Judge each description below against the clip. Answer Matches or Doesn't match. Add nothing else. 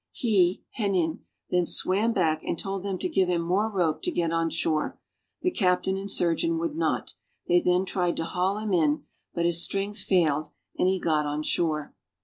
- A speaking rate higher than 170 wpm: Matches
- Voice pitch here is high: Doesn't match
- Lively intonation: Doesn't match